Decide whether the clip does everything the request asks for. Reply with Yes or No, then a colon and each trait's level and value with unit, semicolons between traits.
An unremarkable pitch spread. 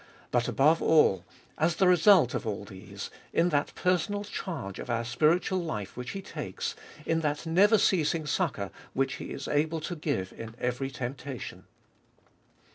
No: wide, 5.9 semitones